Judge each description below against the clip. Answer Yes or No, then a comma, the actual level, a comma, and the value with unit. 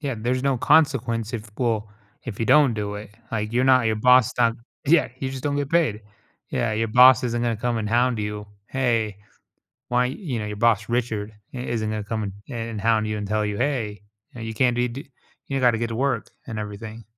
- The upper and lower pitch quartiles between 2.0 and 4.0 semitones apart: Yes, average, 2.8 semitones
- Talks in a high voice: No, low, 115 Hz